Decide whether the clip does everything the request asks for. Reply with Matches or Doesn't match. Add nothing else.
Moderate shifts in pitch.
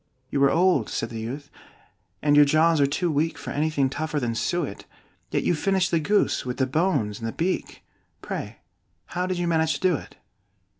Matches